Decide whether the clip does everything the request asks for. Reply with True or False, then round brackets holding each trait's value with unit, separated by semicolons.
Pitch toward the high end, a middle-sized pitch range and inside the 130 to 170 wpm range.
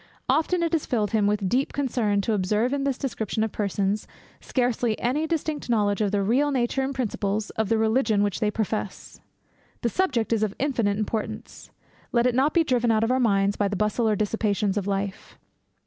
False (220 Hz; 3.8 semitones; 200 wpm)